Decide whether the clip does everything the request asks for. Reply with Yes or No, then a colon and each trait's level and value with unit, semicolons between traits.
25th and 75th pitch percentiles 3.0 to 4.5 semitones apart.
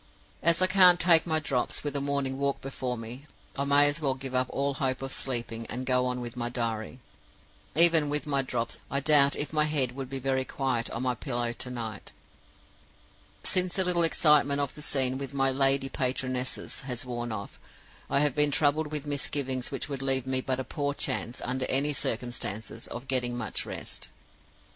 No: narrow, 2.4 semitones